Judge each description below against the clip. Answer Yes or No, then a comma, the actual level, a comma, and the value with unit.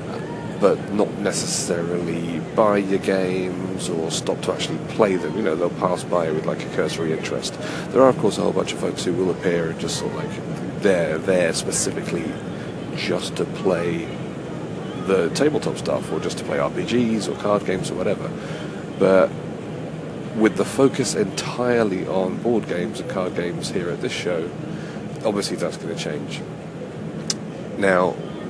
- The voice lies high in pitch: No, very low, 95 Hz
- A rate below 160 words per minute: No, average, 165 wpm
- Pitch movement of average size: Yes, average, 3.1 semitones